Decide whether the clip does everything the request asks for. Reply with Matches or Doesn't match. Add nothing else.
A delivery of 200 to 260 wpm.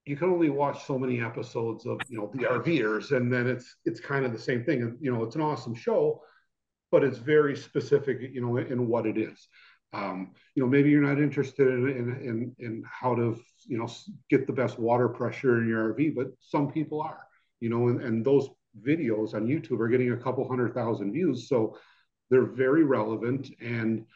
Matches